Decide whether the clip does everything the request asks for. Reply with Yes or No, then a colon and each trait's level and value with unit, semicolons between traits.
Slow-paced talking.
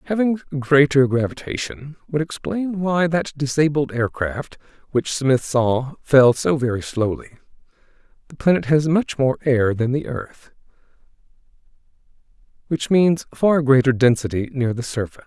Yes: slow, 130 wpm